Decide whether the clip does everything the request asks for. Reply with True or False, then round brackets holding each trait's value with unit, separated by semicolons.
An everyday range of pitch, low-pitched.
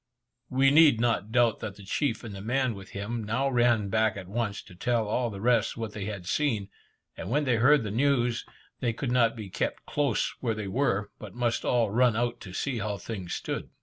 True (3.1 semitones; 115 Hz)